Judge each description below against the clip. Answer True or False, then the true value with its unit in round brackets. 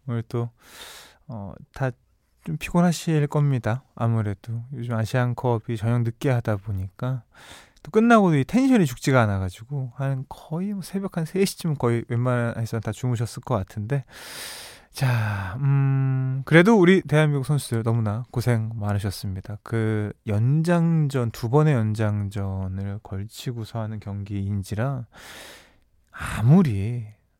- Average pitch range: True (4.5 semitones)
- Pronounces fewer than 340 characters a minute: True (270 characters per minute)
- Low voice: True (120 Hz)